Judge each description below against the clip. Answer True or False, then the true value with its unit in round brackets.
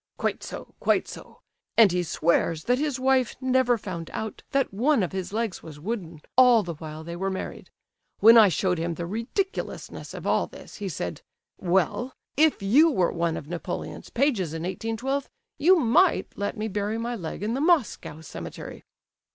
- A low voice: False (210 Hz)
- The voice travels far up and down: True (6.8 semitones)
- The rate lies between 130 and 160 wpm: False (180 wpm)